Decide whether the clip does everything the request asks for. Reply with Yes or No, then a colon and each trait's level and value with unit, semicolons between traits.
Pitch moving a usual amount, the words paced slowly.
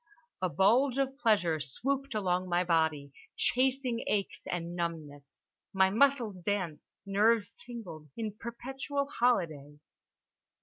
No: wide, 6.3 semitones; slow, 115 wpm